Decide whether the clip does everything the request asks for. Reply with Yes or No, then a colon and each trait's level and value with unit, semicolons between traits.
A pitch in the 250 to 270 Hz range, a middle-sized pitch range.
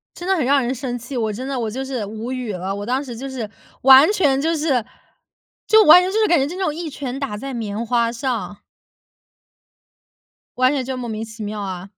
Yes: very high, 255 Hz; average, 3.9 semitones